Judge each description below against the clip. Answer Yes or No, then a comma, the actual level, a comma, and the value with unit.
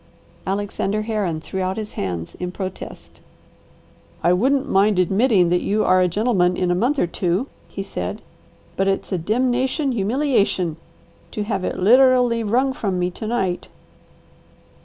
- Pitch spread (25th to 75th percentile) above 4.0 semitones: Yes, average, 4.6 semitones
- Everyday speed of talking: Yes, average, 155 wpm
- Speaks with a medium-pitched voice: No, high, 200 Hz